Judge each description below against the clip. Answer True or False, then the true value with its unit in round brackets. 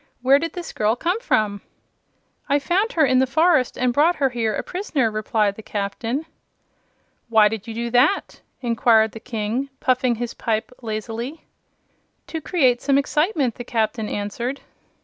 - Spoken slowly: False (160 wpm)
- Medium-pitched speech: False (245 Hz)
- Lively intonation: False (4.4 semitones)